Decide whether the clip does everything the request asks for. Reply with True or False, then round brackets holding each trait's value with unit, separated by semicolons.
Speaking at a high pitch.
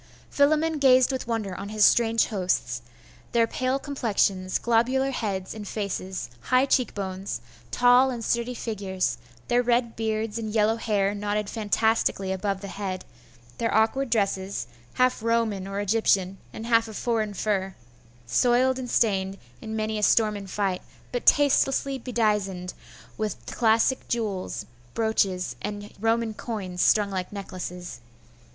True (215 Hz)